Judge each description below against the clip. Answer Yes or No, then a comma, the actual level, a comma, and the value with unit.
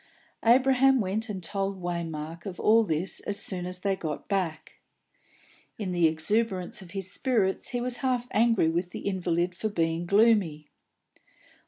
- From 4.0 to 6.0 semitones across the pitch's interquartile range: Yes, average, 4.4 semitones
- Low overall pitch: No, high, 190 Hz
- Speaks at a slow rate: No, average, 155 wpm